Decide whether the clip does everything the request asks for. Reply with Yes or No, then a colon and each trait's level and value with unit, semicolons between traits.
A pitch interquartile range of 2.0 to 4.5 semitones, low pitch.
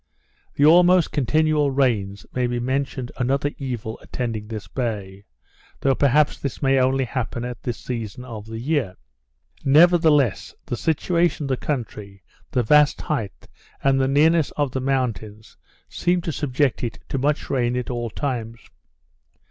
Yes: average, 3.8 semitones; low, 130 Hz